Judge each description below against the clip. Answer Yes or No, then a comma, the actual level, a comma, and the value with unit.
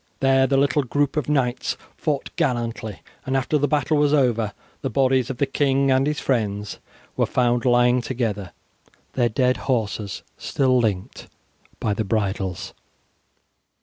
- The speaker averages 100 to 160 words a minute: Yes, average, 150 wpm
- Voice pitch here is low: Yes, low, 125 Hz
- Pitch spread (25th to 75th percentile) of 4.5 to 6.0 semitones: No, average, 3.5 semitones